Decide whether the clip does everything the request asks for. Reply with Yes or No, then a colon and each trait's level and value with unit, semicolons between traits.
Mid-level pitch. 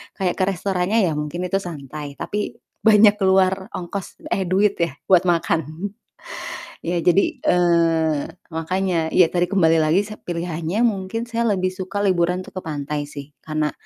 Yes: medium, 180 Hz